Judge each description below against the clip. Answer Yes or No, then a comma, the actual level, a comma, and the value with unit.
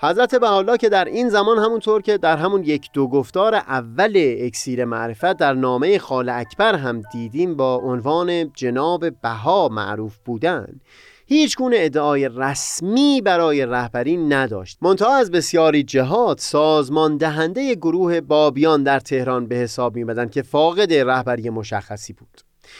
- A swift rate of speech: No, average, 140 wpm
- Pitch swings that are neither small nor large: No, wide, 6.0 semitones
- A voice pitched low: No, medium, 150 Hz